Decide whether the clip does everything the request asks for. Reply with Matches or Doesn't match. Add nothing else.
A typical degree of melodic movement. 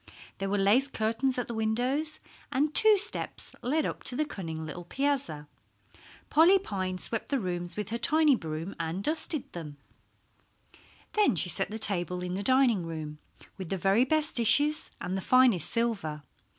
Doesn't match